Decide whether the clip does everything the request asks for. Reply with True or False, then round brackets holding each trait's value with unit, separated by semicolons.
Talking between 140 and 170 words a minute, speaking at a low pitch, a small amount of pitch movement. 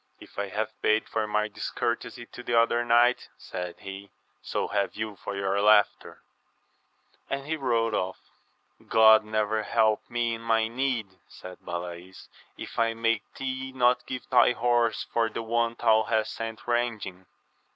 True (160 wpm; 115 Hz; 2.3 semitones)